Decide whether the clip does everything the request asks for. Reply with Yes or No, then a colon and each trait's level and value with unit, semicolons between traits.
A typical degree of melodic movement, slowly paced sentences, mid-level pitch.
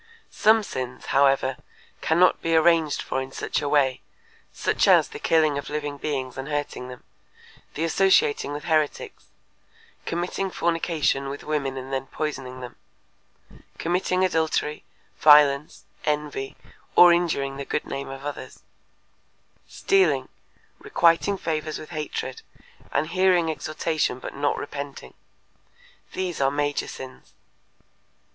Yes: average, 3.3 semitones; slow, 125 wpm; medium, 150 Hz